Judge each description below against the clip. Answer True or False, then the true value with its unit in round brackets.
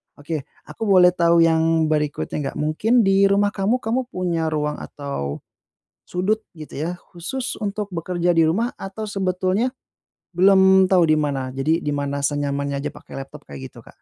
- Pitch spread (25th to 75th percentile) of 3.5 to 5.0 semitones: True (4.6 semitones)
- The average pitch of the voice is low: False (170 Hz)